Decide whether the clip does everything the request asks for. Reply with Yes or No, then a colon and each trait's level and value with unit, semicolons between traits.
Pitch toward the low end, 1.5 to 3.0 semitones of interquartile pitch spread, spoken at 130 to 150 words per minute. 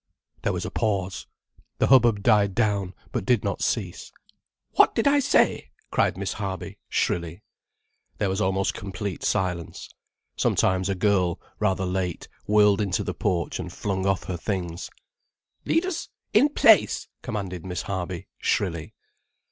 Yes: very low, 95 Hz; narrow, 2.5 semitones; average, 140 wpm